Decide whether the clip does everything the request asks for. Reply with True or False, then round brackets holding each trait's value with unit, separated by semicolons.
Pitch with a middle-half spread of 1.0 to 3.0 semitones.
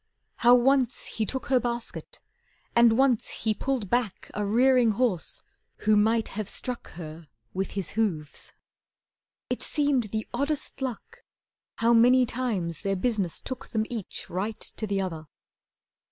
False (4.1 semitones)